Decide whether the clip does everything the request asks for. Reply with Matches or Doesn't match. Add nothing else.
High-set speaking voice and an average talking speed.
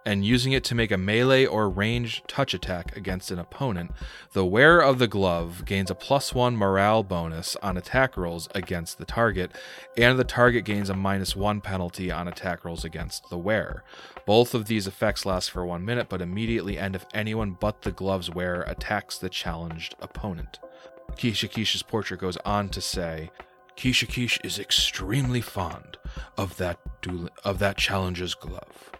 Doesn't match